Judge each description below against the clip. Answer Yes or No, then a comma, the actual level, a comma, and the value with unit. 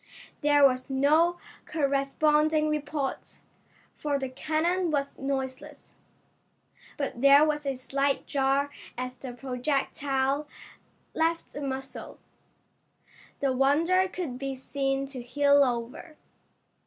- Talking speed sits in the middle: No, slow, 105 wpm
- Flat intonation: Yes, narrow, 2.2 semitones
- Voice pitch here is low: No, very high, 280 Hz